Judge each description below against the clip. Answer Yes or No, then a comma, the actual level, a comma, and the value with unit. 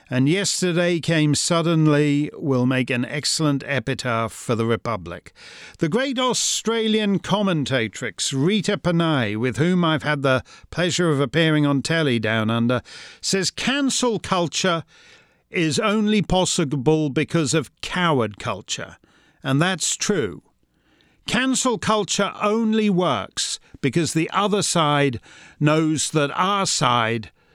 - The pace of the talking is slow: Yes, slow, 120 wpm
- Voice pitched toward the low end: No, medium, 155 Hz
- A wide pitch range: Yes, wide, 5.8 semitones